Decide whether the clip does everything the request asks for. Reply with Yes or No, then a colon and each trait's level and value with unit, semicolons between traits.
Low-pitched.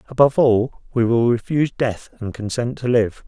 Yes: low, 120 Hz